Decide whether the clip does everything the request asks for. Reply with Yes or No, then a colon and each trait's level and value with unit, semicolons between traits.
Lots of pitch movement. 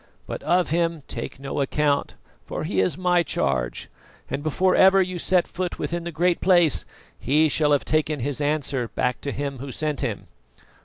No: average, 3.8 semitones